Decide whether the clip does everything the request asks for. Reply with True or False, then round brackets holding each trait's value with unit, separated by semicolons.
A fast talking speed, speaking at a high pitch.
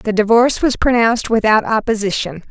False (145 wpm; 225 Hz)